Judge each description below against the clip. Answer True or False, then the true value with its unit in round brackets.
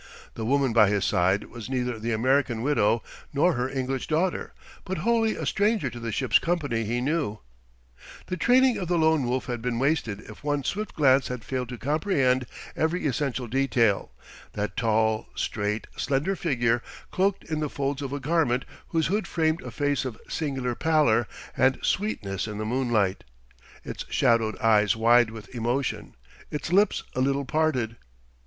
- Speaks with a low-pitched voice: True (130 Hz)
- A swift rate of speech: False (170 wpm)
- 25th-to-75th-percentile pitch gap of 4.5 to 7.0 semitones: True (5.1 semitones)